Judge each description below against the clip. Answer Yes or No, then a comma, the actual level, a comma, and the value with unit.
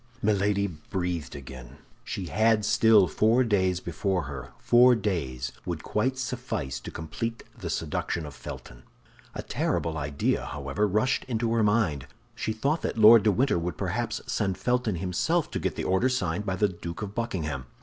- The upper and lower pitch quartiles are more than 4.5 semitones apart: Yes, wide, 5.5 semitones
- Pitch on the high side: No, low, 100 Hz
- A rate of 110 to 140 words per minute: No, average, 170 wpm